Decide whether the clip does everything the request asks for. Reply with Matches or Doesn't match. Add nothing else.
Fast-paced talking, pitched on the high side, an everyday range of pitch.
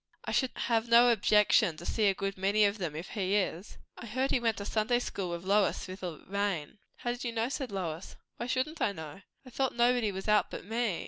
Matches